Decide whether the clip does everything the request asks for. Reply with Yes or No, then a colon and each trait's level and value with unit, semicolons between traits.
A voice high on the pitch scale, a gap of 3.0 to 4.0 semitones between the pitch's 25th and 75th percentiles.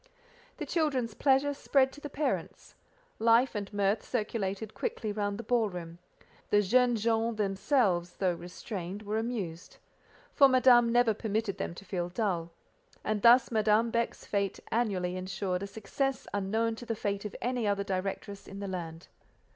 Yes: high, 210 Hz; average, 3.4 semitones